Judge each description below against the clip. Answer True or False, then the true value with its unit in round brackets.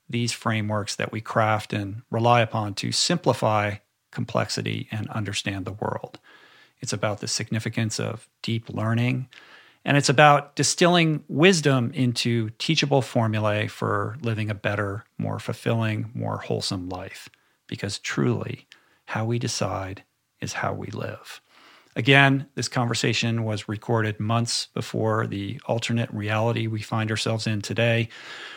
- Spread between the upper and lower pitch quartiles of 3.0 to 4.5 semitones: False (2.4 semitones)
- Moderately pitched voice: False (115 Hz)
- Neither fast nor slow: False (130 wpm)